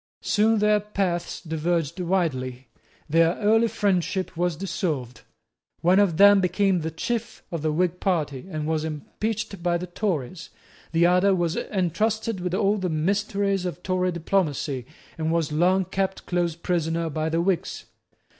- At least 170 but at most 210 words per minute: No, average, 150 wpm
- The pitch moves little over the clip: No, average, 3.4 semitones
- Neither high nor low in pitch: Yes, medium, 175 Hz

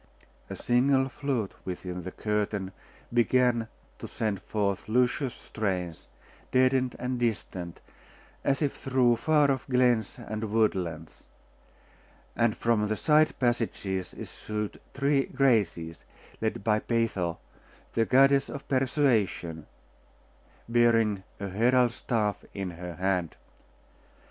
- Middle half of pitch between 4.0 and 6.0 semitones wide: Yes, average, 4.6 semitones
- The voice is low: Yes, low, 115 Hz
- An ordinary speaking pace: No, slow, 110 wpm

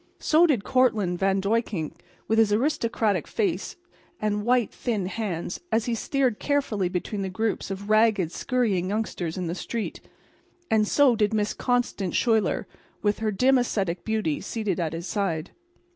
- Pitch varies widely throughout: No, average, 3.4 semitones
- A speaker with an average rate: Yes, average, 160 wpm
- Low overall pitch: No, high, 210 Hz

